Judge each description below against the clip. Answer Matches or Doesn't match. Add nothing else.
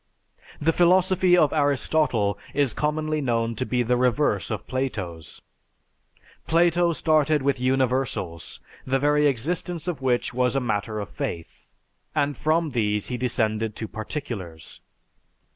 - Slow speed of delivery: Matches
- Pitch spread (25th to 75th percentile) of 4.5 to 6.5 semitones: Matches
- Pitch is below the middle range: Matches